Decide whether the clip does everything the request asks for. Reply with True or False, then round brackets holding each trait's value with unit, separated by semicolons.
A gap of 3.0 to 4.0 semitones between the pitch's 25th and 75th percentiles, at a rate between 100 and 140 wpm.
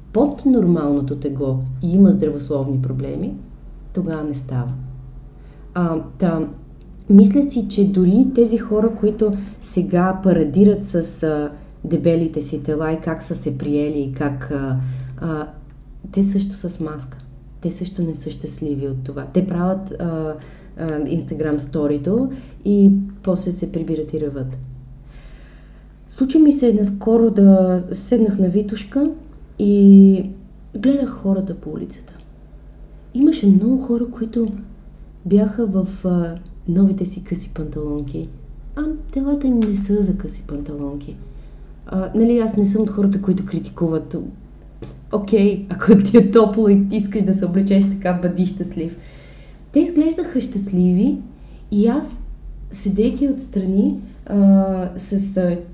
False (5.1 semitones; 130 wpm)